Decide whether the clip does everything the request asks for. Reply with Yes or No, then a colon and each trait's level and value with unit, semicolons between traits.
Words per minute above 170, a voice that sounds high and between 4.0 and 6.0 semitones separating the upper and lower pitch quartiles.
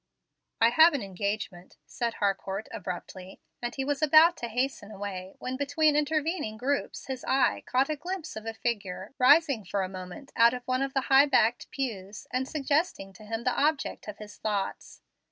Yes: average, 185 wpm; high, 245 Hz; wide, 5.5 semitones